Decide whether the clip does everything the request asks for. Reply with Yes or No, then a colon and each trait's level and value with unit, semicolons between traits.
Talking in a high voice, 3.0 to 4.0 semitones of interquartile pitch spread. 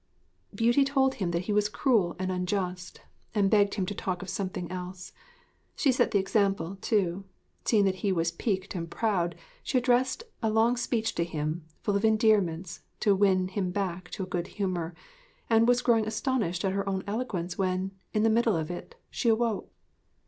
Yes: high, 195 Hz; average, 3.5 semitones